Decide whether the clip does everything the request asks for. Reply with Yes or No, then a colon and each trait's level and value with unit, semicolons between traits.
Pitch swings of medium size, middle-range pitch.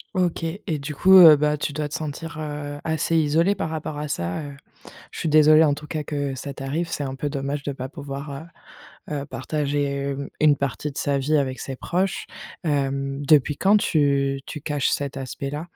No: narrow, 1.9 semitones; medium, 145 Hz